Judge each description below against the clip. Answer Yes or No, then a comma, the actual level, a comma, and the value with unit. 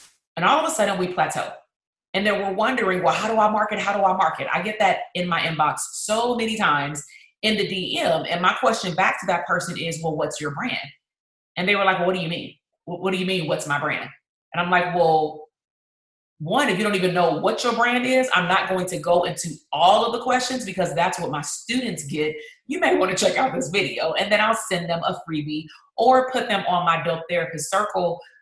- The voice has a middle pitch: Yes, medium, 180 Hz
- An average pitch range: Yes, average, 4.5 semitones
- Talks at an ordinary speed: No, fast, 240 wpm